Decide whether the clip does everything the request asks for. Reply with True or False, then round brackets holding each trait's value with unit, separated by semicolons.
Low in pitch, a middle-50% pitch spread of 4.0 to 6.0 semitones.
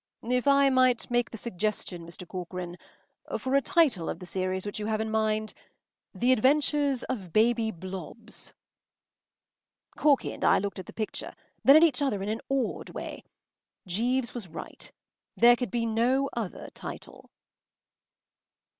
False (225 Hz; 4.8 semitones)